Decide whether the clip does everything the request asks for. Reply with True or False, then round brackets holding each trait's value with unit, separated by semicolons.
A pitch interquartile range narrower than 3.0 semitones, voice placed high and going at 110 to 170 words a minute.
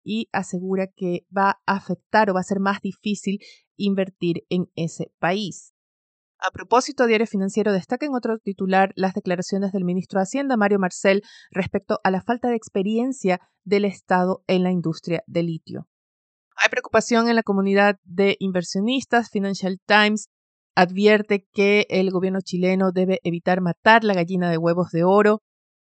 True (2.4 semitones; 195 Hz; 160 wpm)